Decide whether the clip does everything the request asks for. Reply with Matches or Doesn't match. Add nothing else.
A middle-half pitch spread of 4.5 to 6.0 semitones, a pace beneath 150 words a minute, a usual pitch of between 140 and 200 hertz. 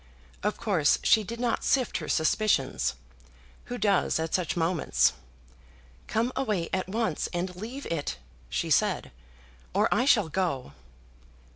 Matches